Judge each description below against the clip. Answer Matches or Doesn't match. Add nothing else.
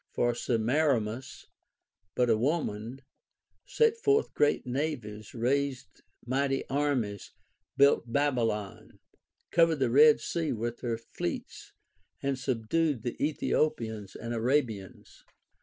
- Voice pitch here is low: Matches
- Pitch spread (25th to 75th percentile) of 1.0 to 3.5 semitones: Doesn't match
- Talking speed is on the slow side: Matches